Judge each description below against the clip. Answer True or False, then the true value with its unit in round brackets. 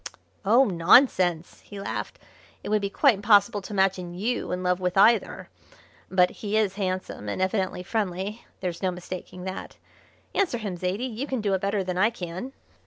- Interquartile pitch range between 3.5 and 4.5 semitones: False (2.9 semitones)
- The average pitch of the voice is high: True (195 Hz)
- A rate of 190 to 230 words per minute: False (175 wpm)